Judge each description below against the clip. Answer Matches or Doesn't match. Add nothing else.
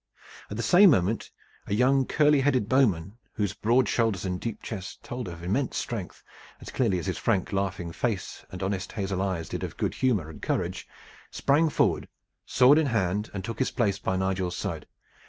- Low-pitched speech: Matches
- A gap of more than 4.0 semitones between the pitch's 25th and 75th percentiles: Matches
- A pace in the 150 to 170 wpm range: Doesn't match